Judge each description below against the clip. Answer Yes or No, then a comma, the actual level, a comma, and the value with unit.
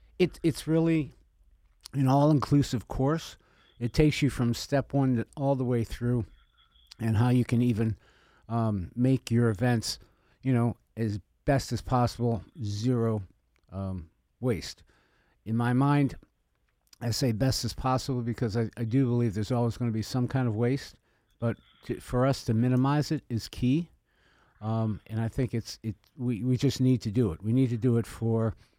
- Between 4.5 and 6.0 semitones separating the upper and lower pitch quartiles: No, average, 2.7 semitones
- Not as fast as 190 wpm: Yes, average, 175 wpm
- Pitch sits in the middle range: No, low, 120 Hz